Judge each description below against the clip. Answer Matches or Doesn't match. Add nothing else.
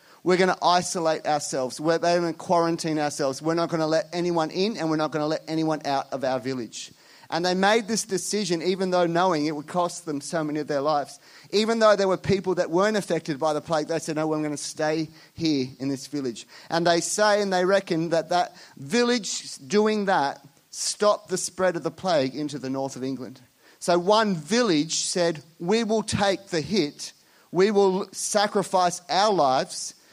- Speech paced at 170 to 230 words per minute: Matches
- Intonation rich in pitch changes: Doesn't match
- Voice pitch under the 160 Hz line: Doesn't match